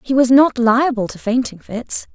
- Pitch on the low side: No, high, 245 Hz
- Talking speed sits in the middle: Yes, average, 195 wpm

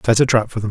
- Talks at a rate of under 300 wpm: No, fast, 425 wpm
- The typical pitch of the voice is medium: No, low, 115 Hz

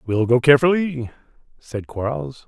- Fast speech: No, slow, 120 wpm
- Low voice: Yes, low, 130 Hz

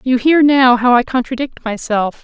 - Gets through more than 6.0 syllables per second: No, 4.7 syllables/s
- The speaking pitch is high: Yes, very high, 250 Hz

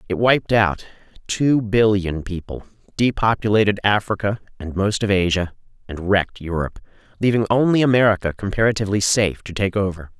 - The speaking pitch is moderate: No, low, 100 Hz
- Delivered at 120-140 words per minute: Yes, slow, 135 wpm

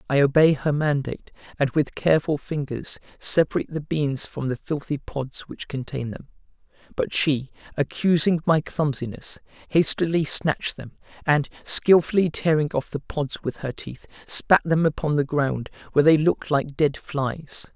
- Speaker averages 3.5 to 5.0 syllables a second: Yes, 4.7 syllables/s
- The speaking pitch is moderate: Yes, medium, 145 Hz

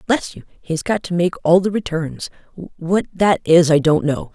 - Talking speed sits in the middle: No, fast, 220 wpm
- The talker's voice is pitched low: No, medium, 170 Hz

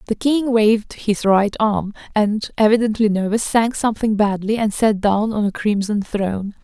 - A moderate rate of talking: Yes, average, 170 wpm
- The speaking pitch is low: No, high, 215 Hz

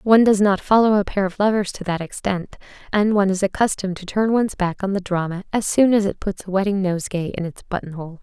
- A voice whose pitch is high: Yes, high, 195 Hz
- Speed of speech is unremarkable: No, fast, 240 wpm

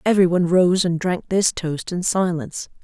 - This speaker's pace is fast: No, average, 170 wpm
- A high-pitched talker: No, medium, 180 Hz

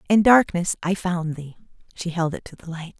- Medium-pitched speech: Yes, medium, 175 Hz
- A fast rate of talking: Yes, fast, 220 wpm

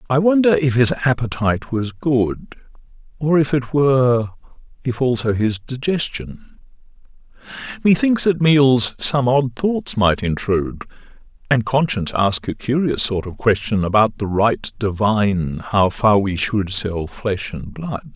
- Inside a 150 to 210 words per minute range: No, average, 140 wpm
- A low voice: Yes, low, 120 Hz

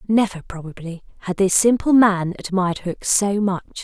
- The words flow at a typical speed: Yes, average, 155 wpm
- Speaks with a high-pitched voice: Yes, high, 195 Hz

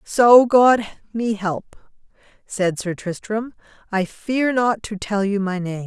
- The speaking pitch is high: Yes, high, 210 Hz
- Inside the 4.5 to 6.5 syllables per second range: No, 3.5 syllables/s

